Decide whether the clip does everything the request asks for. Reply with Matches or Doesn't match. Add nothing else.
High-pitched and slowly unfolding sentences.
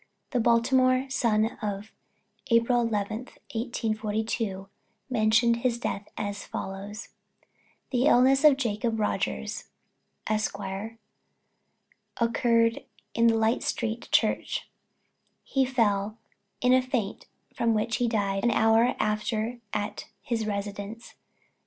Matches